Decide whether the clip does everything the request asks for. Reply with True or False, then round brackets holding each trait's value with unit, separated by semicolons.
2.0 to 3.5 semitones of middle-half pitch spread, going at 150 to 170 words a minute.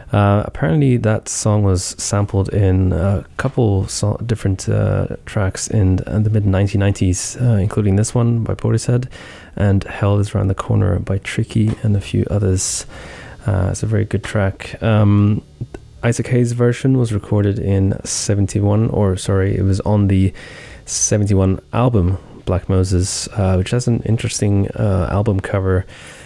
True (2.6 semitones; 155 wpm)